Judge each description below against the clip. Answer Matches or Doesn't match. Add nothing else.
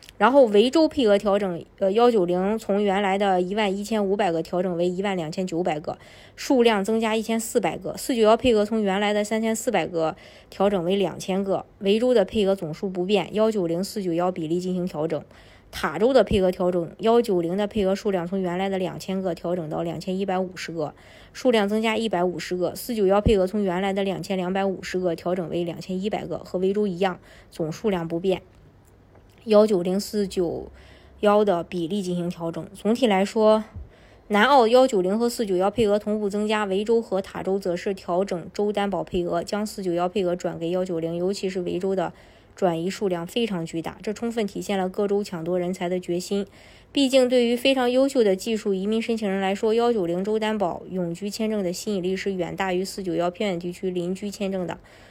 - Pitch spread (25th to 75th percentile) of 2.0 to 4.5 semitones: Matches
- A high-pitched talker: Matches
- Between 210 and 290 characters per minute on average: Doesn't match